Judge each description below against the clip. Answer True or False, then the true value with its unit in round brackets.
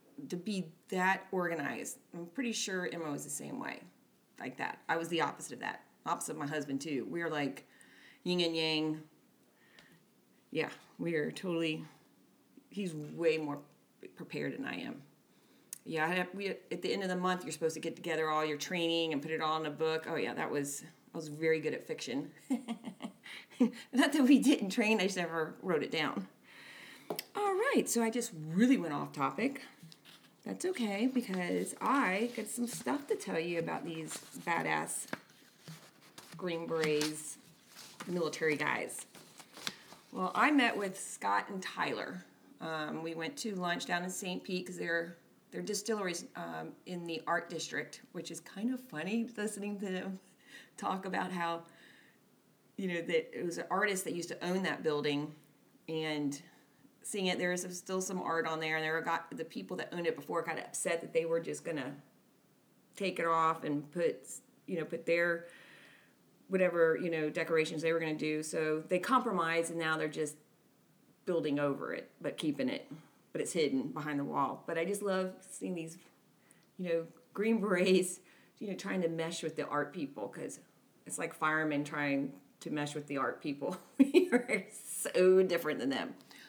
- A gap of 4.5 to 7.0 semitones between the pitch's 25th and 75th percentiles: False (3.8 semitones)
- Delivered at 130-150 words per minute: False (180 wpm)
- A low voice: False (170 Hz)